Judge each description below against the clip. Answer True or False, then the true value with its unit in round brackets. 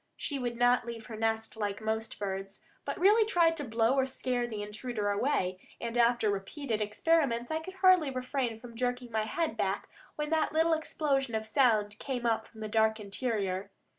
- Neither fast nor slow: True (190 wpm)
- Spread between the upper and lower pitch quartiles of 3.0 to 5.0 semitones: True (4.0 semitones)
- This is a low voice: False (235 Hz)